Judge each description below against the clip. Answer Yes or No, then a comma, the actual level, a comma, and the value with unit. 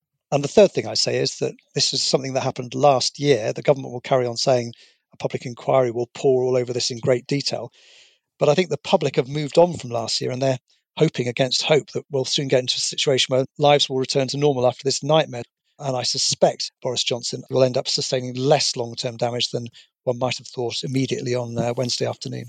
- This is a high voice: No, low, 130 Hz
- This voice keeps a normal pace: No, fast, 230 wpm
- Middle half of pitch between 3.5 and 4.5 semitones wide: No, narrow, 2.5 semitones